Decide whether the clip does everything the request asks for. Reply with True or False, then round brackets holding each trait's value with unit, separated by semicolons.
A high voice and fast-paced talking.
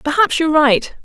False (310 Hz; 175 wpm)